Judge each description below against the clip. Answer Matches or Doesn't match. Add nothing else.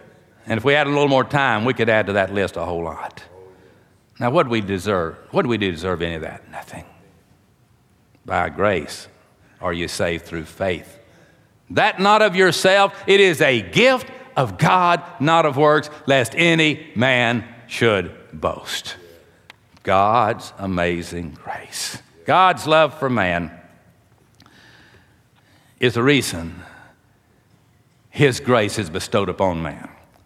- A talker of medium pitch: Doesn't match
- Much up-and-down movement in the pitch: Matches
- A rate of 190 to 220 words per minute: Doesn't match